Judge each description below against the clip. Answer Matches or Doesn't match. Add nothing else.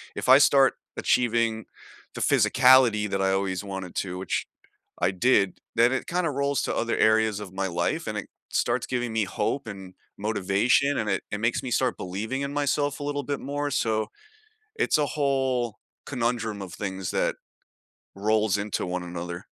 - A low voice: Matches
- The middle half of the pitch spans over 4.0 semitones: Matches